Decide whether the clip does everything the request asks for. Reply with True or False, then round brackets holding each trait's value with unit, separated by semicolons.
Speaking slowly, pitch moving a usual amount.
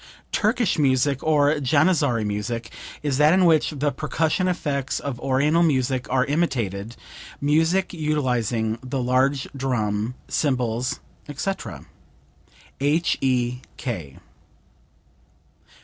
True (95 wpm; 3.8 semitones)